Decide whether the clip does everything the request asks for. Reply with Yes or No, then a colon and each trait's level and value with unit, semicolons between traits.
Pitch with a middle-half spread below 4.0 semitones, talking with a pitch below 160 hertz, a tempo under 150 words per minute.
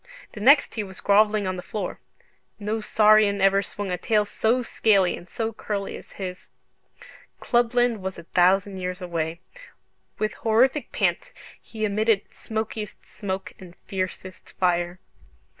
No: average, 2.8 semitones; high, 200 Hz; average, 140 wpm